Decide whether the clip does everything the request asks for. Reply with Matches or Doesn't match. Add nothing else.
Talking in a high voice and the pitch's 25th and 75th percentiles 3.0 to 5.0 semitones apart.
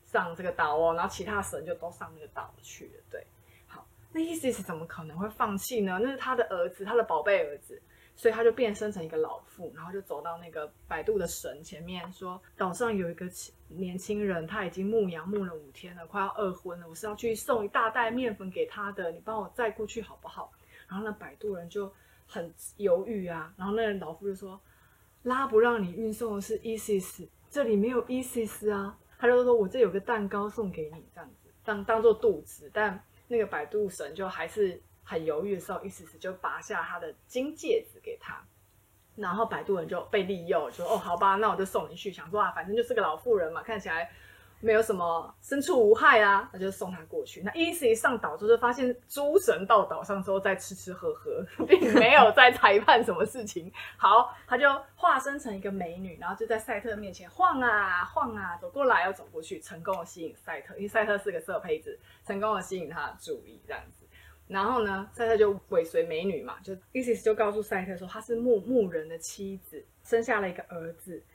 Matches